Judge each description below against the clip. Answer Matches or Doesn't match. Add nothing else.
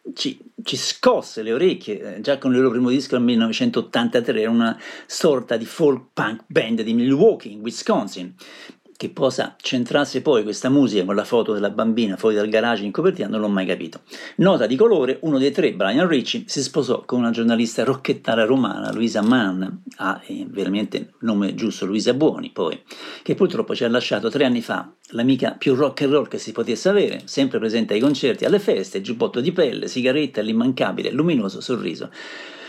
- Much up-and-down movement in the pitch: Doesn't match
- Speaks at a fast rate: Matches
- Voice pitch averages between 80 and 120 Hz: Doesn't match